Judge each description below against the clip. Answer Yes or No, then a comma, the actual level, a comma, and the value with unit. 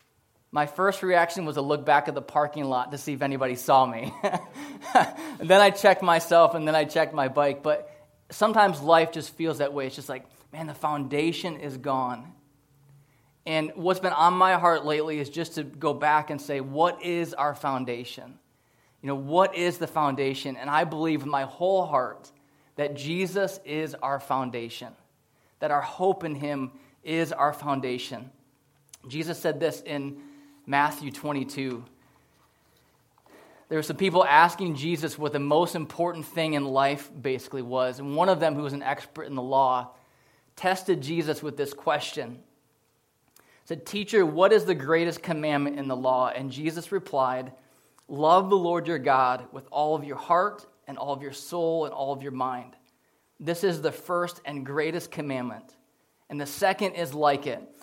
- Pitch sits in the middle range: Yes, medium, 150 Hz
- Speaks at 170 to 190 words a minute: Yes, average, 175 wpm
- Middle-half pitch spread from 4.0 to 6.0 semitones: No, average, 3.4 semitones